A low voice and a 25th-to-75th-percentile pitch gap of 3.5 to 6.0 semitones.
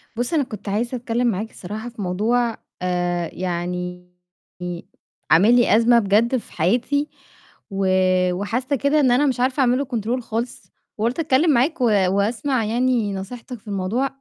No: high, 230 Hz; average, 4.2 semitones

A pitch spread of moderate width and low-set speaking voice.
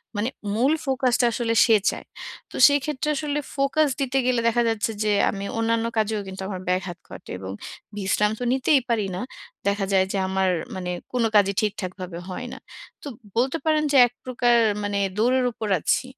No: average, 4.6 semitones; high, 225 Hz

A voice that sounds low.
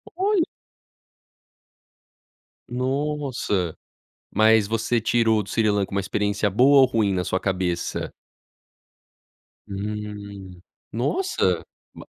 Yes: low, 105 Hz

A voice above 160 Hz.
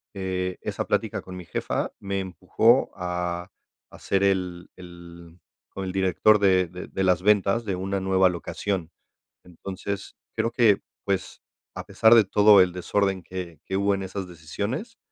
No: very low, 95 Hz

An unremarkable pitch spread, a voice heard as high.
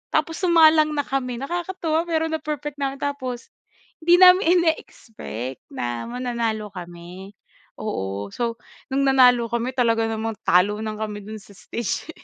No: wide, 6.4 semitones; high, 245 Hz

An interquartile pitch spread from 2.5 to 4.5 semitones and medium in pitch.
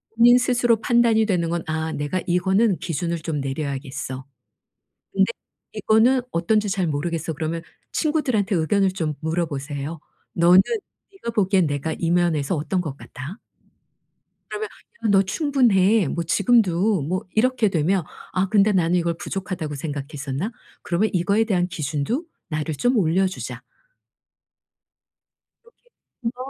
No: average, 5.3 semitones; medium, 180 Hz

